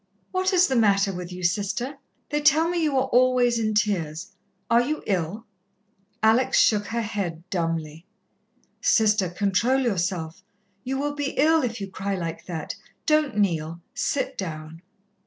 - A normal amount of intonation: No, wide, 6.7 semitones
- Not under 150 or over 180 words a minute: Yes, average, 155 wpm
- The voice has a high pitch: Yes, high, 210 Hz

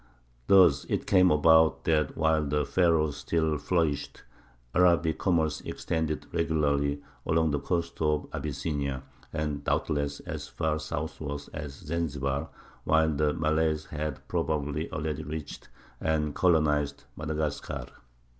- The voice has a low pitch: Yes, very low, 75 Hz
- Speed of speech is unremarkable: No, slow, 115 wpm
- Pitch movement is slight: Yes, narrow, 1.7 semitones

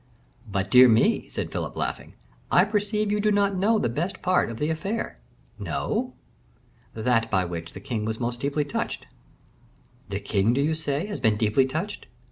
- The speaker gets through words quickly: No, average, 180 wpm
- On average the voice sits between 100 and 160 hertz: Yes, medium, 140 Hz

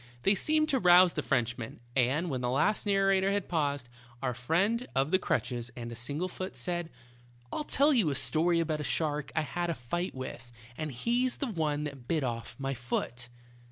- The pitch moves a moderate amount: No, wide, 6.4 semitones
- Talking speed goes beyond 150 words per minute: Yes, average, 195 wpm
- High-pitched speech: No, medium, 155 Hz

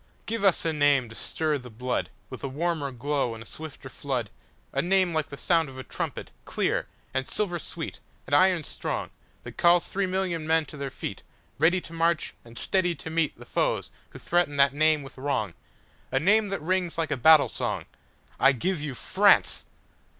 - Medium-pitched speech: Yes, medium, 155 Hz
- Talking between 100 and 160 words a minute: No, average, 170 wpm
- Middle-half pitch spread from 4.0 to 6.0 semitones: Yes, average, 4.3 semitones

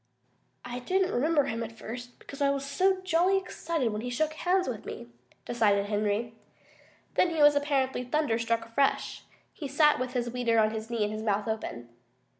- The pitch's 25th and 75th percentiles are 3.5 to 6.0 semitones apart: Yes, average, 5.0 semitones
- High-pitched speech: Yes, high, 245 Hz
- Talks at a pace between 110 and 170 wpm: No, average, 185 wpm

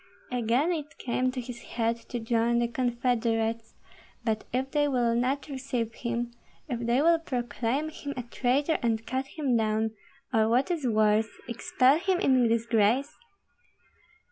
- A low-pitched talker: No, high, 245 Hz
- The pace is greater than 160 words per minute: No, average, 150 wpm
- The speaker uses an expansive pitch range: No, average, 2.8 semitones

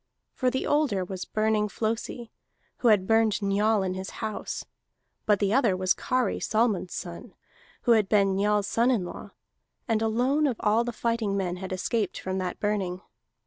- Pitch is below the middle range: No, high, 210 Hz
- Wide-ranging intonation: No, average, 3.3 semitones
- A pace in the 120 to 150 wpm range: No, average, 175 wpm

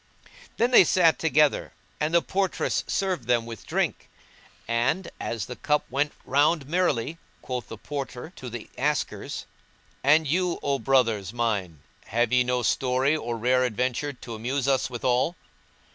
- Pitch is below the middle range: Yes, low, 130 Hz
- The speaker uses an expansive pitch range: No, average, 4.2 semitones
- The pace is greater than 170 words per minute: No, average, 150 wpm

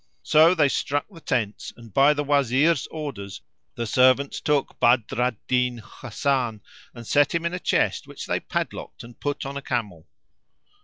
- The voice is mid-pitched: No, low, 130 Hz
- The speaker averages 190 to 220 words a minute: No, average, 170 wpm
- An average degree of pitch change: Yes, average, 3.6 semitones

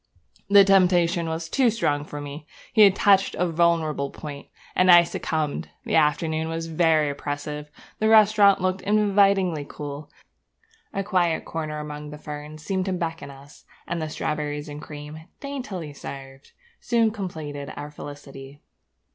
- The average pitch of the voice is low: No, medium, 160 Hz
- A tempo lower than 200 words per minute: Yes, average, 145 wpm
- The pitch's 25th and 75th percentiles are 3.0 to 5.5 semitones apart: Yes, average, 4.1 semitones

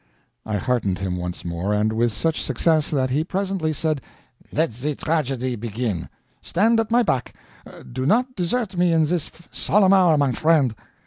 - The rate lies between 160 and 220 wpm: Yes, average, 170 wpm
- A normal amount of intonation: No, wide, 6.9 semitones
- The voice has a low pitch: No, medium, 150 Hz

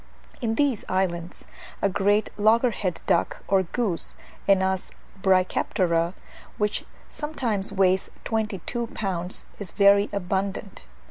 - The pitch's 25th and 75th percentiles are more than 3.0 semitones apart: No, narrow, 2.4 semitones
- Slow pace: Yes, slow, 110 wpm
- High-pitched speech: Yes, high, 195 Hz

